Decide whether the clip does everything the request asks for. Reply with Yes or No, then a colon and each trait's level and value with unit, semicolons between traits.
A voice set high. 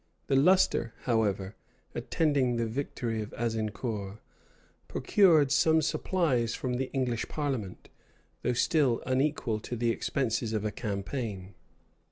No: low, 120 Hz